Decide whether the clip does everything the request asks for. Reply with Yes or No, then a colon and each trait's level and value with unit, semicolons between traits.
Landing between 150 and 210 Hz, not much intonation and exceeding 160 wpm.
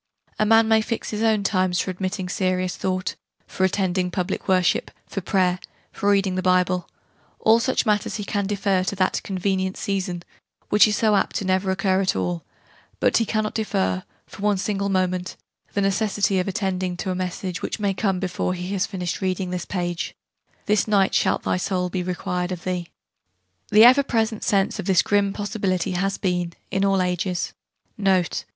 Yes: high, 190 Hz; narrow, 1.9 semitones; average, 185 wpm